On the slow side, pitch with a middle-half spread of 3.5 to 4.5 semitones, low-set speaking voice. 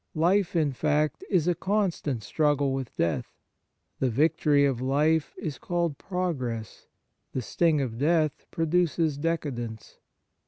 No: slow, 125 wpm; average, 3.9 semitones; medium, 150 Hz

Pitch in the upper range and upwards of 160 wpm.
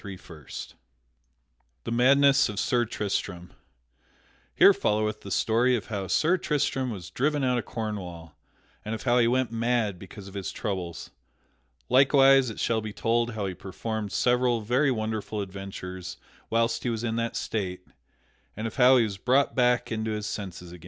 No: low, 110 Hz; average, 170 wpm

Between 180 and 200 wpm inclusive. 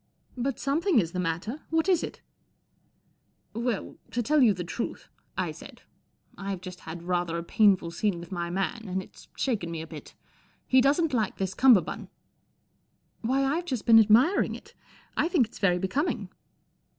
Yes: average, 185 wpm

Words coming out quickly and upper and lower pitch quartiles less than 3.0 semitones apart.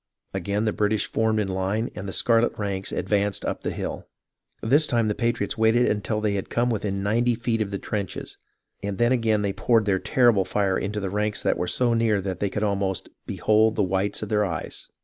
Yes: fast, 220 wpm; narrow, 2.4 semitones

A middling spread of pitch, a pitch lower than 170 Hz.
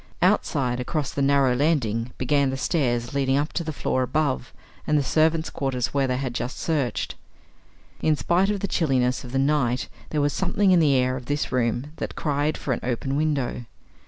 Yes: average, 3.2 semitones; medium, 140 Hz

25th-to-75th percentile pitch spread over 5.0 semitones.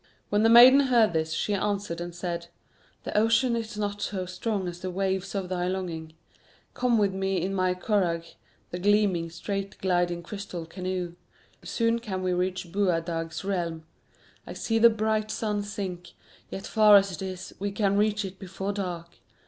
No: average, 2.8 semitones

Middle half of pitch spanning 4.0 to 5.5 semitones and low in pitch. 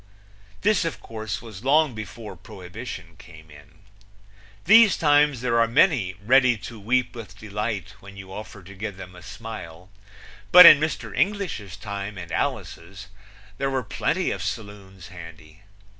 Yes: average, 5.2 semitones; low, 105 Hz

